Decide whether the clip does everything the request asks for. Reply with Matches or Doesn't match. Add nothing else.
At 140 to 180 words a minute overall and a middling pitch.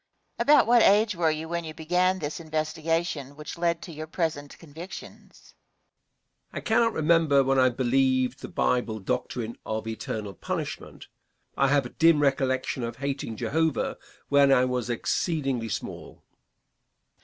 Matches